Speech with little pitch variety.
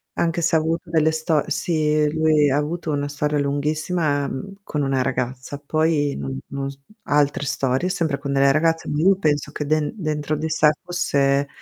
Yes: narrow, 2.1 semitones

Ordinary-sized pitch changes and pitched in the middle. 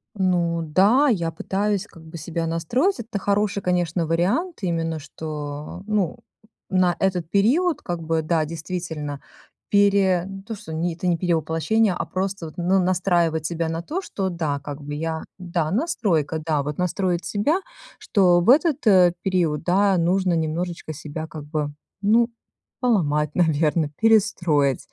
Yes: average, 3.5 semitones; medium, 175 Hz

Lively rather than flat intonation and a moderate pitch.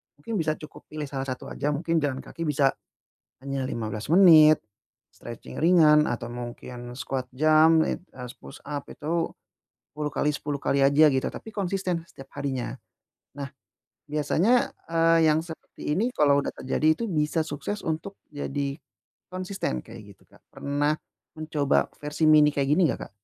No: average, 2.9 semitones; medium, 150 Hz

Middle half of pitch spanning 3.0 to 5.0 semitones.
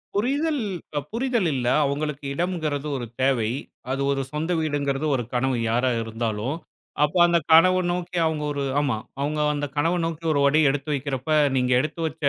Yes: average, 3.8 semitones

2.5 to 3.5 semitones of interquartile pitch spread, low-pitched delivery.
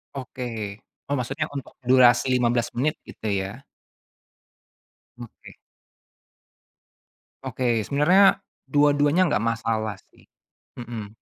No: average, 3.9 semitones; low, 125 Hz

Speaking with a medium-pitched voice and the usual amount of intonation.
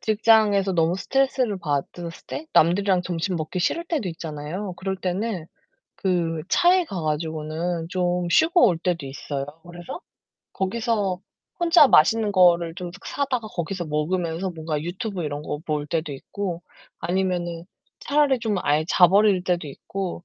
Yes: medium, 180 Hz; average, 3.8 semitones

